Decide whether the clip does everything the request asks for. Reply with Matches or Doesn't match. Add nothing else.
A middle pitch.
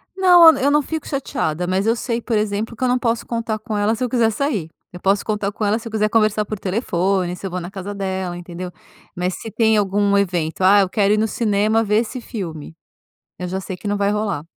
Doesn't match